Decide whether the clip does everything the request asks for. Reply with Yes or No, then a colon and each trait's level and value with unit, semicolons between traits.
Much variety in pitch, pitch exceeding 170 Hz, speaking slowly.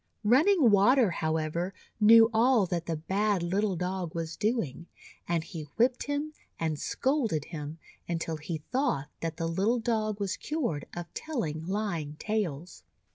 No: wide, 5.8 semitones; high, 190 Hz; average, 145 wpm